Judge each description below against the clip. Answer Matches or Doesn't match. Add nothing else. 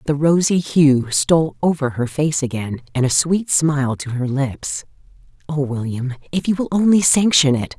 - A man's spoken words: Doesn't match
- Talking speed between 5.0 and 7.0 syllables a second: Doesn't match